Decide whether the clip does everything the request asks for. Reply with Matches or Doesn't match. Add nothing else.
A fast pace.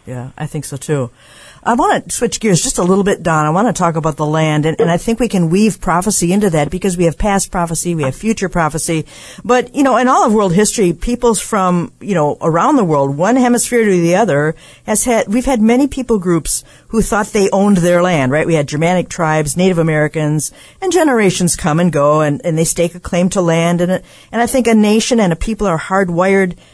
Matches